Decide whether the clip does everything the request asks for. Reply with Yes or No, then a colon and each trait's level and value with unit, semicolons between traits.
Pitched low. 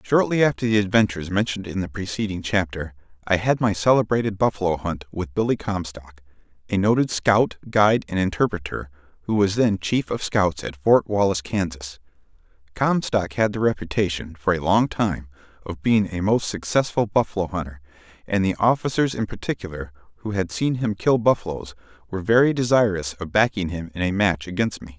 Yes: very low, 95 Hz